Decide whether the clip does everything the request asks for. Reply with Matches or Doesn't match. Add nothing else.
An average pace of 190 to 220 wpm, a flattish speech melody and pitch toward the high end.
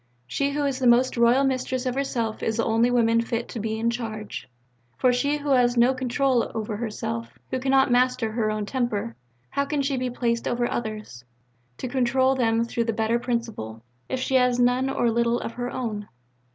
Matches